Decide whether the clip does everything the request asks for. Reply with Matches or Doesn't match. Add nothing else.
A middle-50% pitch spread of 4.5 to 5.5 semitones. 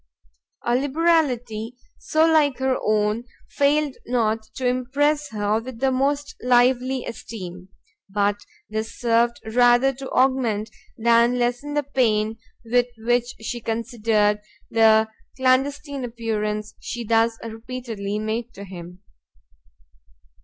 Doesn't match